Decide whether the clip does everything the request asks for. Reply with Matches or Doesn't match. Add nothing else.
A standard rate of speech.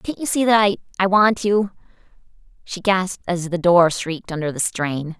Matches